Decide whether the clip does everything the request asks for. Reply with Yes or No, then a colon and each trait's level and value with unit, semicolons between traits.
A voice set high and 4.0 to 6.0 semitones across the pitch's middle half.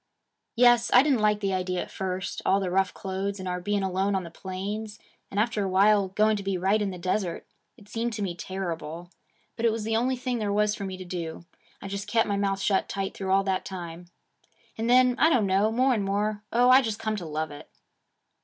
No: high, 200 Hz; narrow, 2.6 semitones